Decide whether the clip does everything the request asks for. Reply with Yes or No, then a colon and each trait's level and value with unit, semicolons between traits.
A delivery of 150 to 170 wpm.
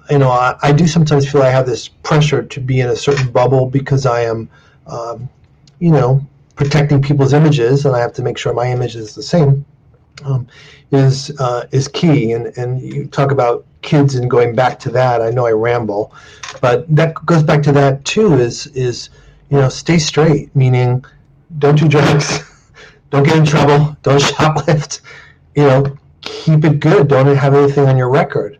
No: average, 190 wpm